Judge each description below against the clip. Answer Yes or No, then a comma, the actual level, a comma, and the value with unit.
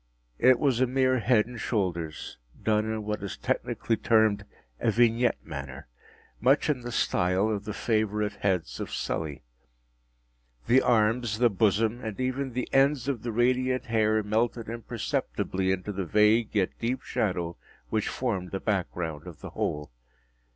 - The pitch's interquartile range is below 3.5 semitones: No, average, 3.9 semitones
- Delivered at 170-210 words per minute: No, average, 160 wpm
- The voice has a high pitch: No, low, 110 Hz